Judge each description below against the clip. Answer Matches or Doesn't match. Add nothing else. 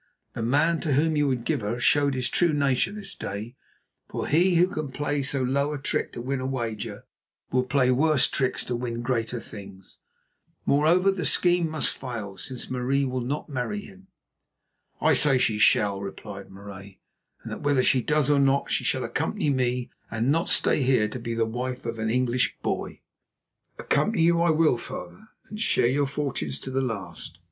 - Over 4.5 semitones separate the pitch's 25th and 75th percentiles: Doesn't match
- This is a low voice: Matches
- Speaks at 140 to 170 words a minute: Doesn't match